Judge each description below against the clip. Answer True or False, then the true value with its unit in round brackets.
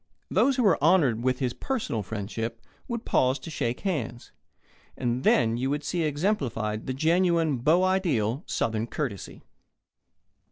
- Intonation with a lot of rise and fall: True (6.6 semitones)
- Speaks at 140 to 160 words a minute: True (145 wpm)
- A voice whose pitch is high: False (135 Hz)